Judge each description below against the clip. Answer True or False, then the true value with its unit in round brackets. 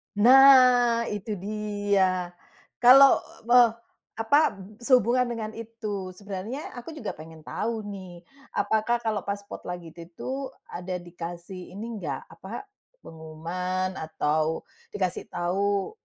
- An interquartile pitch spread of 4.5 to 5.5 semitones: True (4.8 semitones)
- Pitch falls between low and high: False (205 Hz)